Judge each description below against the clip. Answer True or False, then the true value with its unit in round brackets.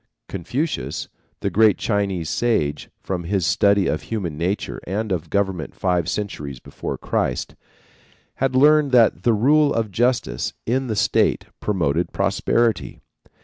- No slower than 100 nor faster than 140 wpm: True (135 wpm)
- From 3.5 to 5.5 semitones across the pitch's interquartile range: True (5.1 semitones)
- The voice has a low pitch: True (100 Hz)